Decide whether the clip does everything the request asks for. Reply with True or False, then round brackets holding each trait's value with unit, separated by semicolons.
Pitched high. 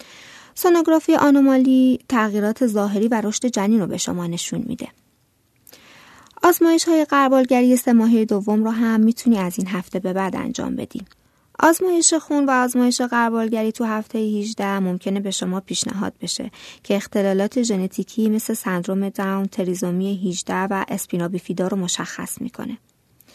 True (220 Hz)